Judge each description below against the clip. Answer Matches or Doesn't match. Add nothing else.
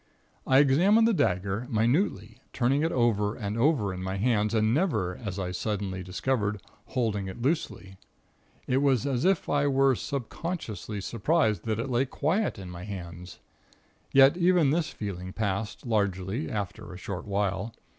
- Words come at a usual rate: Matches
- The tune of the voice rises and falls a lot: Matches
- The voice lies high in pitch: Doesn't match